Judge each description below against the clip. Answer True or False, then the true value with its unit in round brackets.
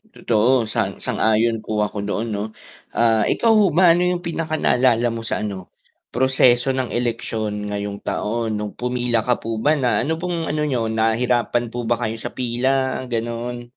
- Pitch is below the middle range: True (120 Hz)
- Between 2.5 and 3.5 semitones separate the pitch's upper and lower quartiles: True (2.8 semitones)